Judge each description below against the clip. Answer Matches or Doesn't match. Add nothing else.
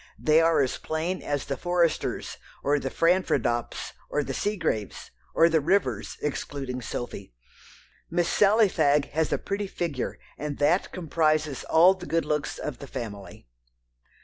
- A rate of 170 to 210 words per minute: Doesn't match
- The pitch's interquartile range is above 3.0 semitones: Matches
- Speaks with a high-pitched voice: Doesn't match